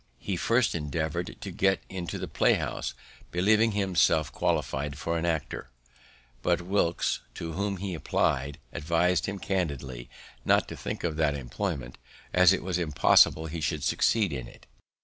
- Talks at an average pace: Yes, average, 155 wpm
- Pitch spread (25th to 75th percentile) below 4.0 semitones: No, average, 4.6 semitones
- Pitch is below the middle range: Yes, very low, 85 Hz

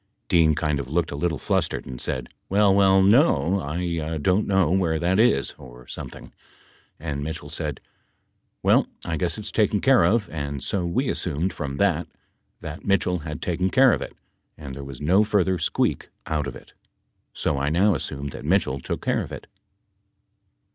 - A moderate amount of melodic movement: Yes, average, 5.0 semitones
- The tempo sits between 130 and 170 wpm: No, average, 180 wpm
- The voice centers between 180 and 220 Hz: No, very low, 85 Hz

